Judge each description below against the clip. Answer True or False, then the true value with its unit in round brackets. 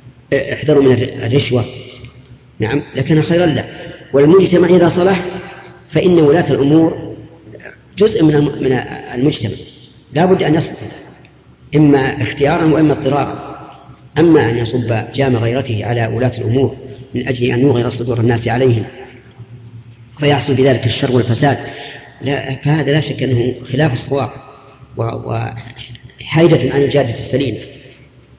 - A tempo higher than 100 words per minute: True (115 wpm)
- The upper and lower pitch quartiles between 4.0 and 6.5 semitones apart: False (2.9 semitones)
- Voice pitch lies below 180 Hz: True (135 Hz)